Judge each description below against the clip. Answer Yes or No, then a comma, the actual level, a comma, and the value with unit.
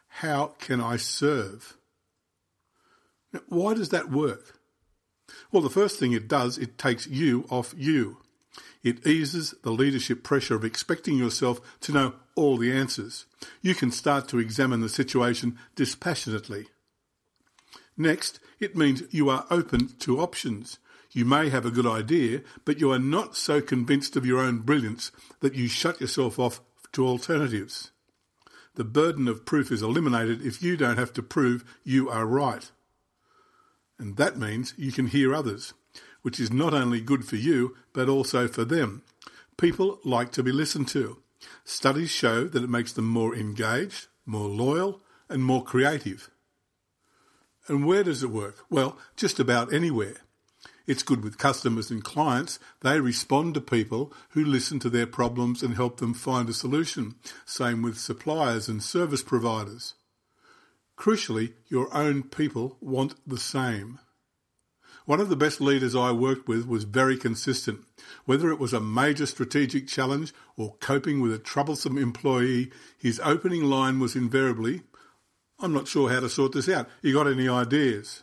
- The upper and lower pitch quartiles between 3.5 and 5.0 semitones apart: No, average, 3.1 semitones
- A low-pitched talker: Yes, low, 130 Hz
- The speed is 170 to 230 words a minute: No, average, 160 wpm